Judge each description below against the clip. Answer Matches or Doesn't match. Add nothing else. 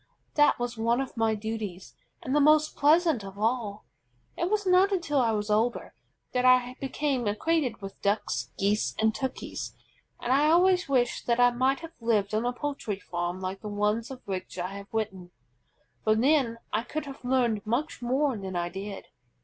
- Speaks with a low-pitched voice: Doesn't match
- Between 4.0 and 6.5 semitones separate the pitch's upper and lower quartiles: Matches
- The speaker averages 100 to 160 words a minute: Doesn't match